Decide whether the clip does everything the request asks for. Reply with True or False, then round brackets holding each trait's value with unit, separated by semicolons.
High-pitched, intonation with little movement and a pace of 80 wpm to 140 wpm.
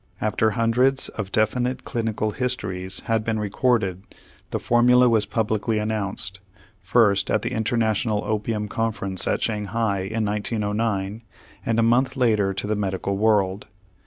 False (110 Hz; 2.2 semitones; 135 wpm)